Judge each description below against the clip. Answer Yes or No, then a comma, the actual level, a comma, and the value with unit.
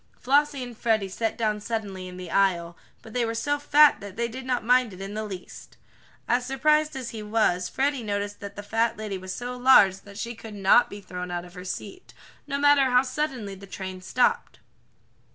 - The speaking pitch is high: Yes, high, 220 Hz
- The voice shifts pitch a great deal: No, average, 4.5 semitones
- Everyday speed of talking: No, fast, 210 wpm